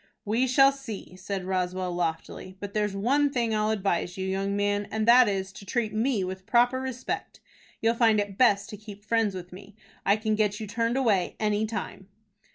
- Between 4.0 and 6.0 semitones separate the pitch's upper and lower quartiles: No, average, 3.1 semitones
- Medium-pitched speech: No, high, 210 Hz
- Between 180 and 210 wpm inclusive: Yes, average, 195 wpm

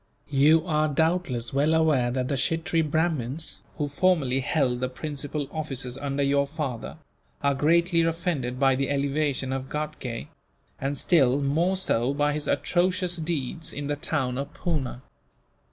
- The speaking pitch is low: No, medium, 145 Hz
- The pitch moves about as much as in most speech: Yes, average, 3.2 semitones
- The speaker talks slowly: No, average, 150 wpm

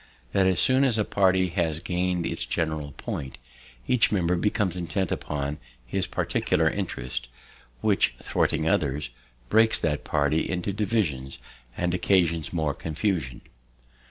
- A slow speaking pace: Yes, slow, 130 wpm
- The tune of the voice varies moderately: Yes, average, 4.3 semitones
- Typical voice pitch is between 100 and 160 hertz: No, very low, 85 Hz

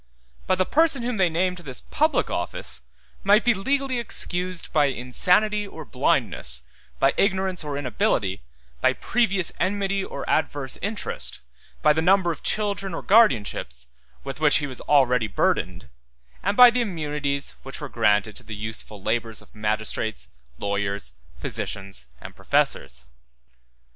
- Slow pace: No, average, 145 wpm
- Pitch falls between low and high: Yes, medium, 160 Hz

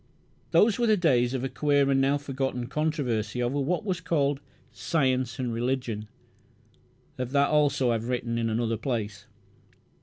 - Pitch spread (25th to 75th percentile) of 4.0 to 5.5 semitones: No, average, 3.3 semitones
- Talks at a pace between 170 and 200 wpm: No, average, 160 wpm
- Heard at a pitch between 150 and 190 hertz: No, low, 130 Hz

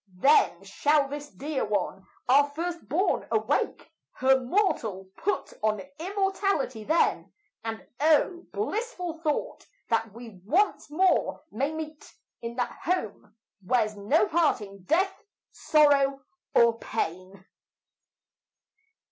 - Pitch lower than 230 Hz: No, very high, 275 Hz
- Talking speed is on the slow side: Yes, slow, 110 wpm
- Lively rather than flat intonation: Yes, wide, 7.1 semitones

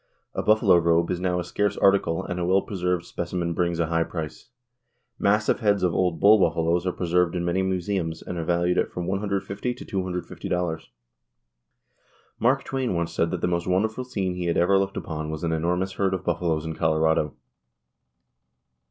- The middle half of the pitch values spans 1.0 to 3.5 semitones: Yes, narrow, 2.5 semitones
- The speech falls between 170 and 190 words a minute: Yes, average, 185 wpm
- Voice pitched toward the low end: Yes, very low, 90 Hz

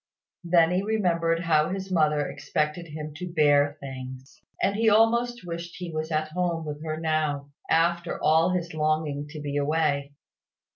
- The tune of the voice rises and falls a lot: No, narrow, 2.6 semitones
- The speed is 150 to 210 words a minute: Yes, average, 160 wpm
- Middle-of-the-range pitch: Yes, medium, 160 Hz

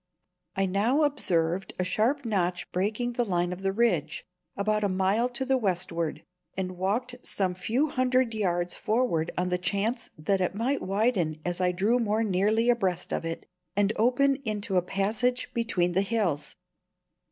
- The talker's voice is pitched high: Yes, high, 200 Hz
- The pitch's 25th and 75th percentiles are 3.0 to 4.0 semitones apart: No, average, 4.6 semitones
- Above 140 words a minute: Yes, average, 165 wpm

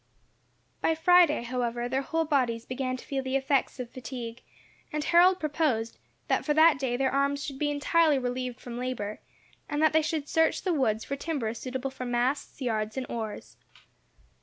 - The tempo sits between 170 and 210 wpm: Yes, average, 180 wpm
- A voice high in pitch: Yes, very high, 265 Hz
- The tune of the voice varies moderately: Yes, average, 3.6 semitones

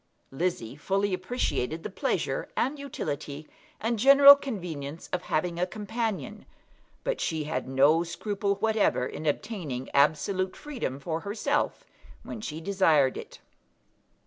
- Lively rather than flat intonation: Yes, wide, 6.3 semitones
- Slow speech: Yes, slow, 125 wpm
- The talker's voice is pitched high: No, medium, 180 Hz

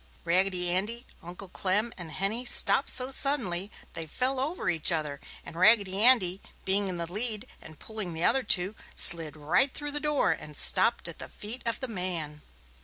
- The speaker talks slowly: No, average, 180 wpm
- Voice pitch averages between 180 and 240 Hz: Yes, high, 190 Hz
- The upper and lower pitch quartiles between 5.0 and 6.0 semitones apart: Yes, wide, 5.6 semitones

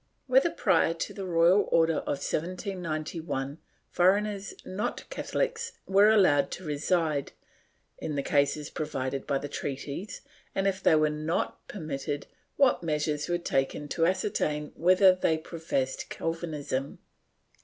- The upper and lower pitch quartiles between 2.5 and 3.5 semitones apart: No, average, 4.2 semitones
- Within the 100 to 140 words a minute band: Yes, slow, 135 wpm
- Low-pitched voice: No, medium, 165 Hz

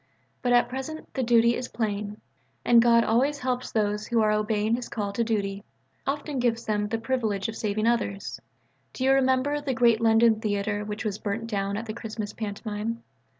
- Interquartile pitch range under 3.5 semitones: Yes, average, 2.7 semitones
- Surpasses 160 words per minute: Yes, average, 190 wpm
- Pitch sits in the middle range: No, high, 225 Hz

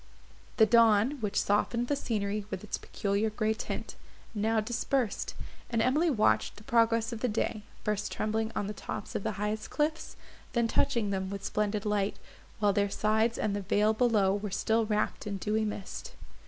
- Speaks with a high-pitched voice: Yes, high, 215 Hz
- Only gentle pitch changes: Yes, narrow, 1.9 semitones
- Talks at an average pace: Yes, average, 180 wpm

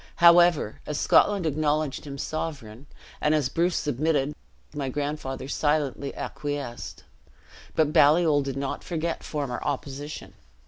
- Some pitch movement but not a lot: No, narrow, 2.2 semitones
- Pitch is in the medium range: Yes, medium, 145 Hz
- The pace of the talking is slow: Yes, slow, 120 wpm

